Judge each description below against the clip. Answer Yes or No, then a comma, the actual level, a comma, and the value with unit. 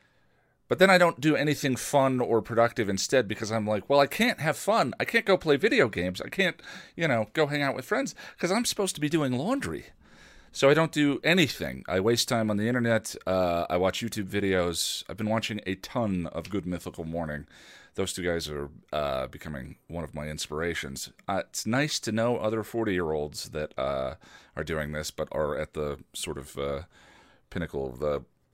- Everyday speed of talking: No, fast, 210 wpm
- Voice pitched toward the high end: No, low, 105 Hz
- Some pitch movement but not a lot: No, wide, 8.3 semitones